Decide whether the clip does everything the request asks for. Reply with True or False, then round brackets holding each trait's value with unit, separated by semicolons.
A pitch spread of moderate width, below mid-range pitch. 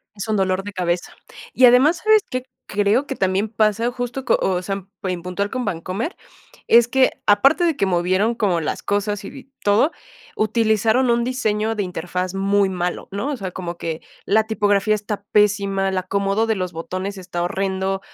False (3.5 semitones; 205 Hz)